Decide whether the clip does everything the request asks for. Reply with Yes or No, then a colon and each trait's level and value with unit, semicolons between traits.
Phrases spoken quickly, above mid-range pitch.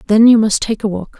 Yes: fast, 300 wpm; high, 215 Hz